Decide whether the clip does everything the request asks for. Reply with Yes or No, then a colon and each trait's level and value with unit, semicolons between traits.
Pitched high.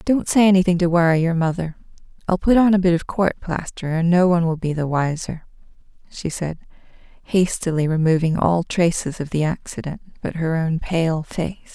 No: medium, 170 Hz